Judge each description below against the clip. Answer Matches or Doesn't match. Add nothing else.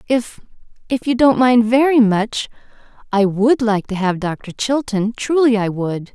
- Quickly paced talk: Doesn't match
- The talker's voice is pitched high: Matches